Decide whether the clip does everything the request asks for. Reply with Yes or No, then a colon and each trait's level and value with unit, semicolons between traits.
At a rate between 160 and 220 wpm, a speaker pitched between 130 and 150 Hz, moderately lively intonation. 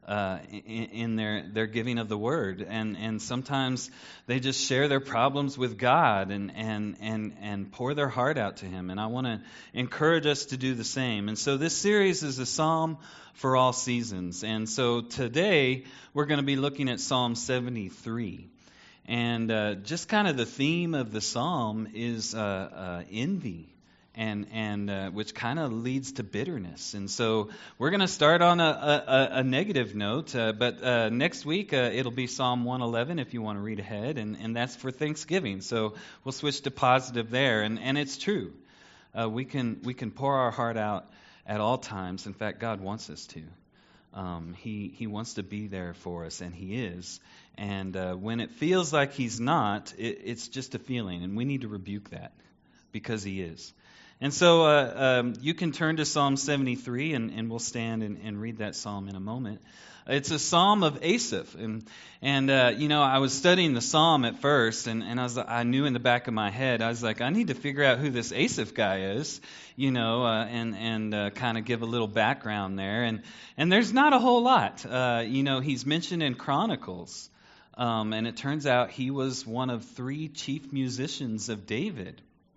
No: fast, 205 wpm; low, 120 Hz; average, 4.2 semitones